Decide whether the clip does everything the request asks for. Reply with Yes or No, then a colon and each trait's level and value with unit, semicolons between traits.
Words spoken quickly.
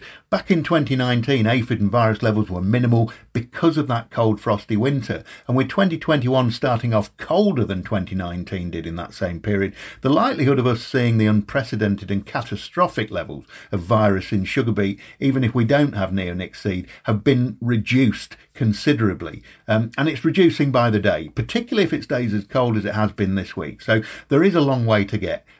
No: average, 190 wpm